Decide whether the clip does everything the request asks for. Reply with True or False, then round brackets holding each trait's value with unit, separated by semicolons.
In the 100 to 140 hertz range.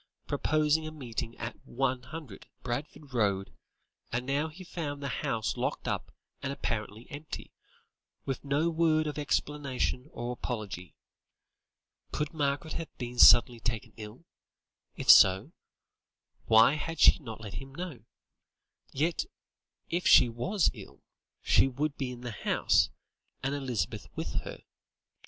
True (135 Hz)